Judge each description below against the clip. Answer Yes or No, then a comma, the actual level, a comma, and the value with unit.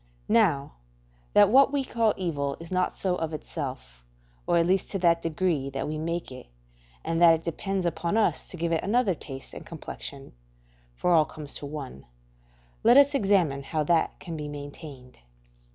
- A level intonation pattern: No, average, 4.5 semitones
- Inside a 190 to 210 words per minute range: No, average, 180 wpm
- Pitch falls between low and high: Yes, medium, 165 Hz